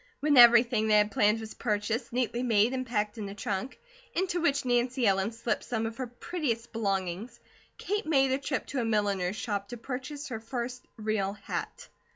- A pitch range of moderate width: Yes, average, 3.5 semitones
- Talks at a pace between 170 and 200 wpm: Yes, average, 190 wpm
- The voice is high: Yes, high, 235 Hz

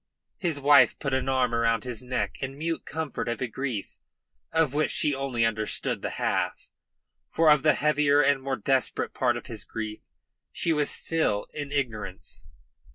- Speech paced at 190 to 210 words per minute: No, average, 170 wpm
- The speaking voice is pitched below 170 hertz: Yes, low, 135 Hz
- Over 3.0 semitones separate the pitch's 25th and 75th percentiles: Yes, average, 4.1 semitones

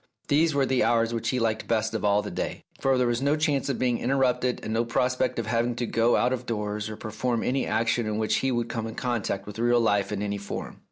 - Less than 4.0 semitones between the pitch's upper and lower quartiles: Yes, narrow, 2.6 semitones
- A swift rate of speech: Yes, fast, 260 wpm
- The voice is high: No, low, 115 Hz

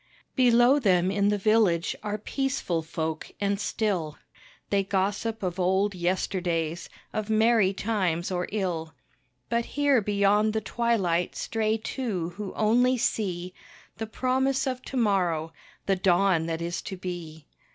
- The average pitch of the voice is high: Yes, high, 200 Hz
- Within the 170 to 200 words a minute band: No, average, 140 wpm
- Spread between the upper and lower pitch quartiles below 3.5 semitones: No, average, 4.1 semitones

